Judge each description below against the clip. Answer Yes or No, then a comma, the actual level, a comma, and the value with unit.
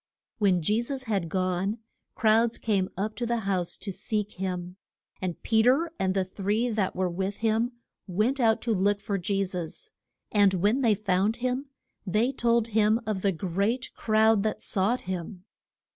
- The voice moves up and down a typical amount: Yes, average, 3.3 semitones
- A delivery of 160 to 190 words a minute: Yes, average, 175 wpm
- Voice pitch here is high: Yes, high, 210 Hz